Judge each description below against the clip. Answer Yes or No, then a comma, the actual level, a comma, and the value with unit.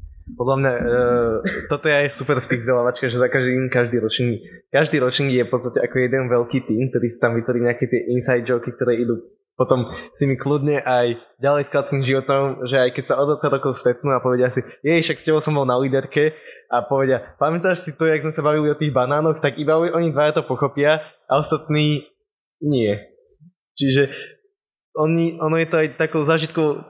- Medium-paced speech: No, fast, 200 wpm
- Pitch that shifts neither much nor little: Yes, average, 3.5 semitones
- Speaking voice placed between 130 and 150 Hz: Yes, medium, 140 Hz